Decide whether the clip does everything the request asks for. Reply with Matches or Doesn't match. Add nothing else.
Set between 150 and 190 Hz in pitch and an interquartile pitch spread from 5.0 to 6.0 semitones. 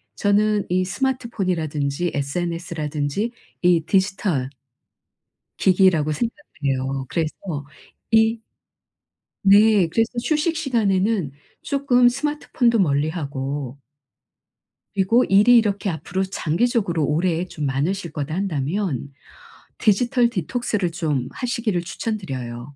Doesn't match